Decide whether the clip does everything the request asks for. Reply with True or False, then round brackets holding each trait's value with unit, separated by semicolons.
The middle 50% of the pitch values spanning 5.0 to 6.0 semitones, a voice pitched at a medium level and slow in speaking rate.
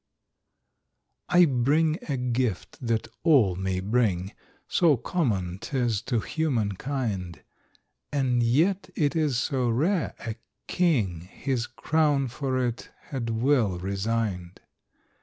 False (5.5 semitones; 125 Hz; 115 wpm)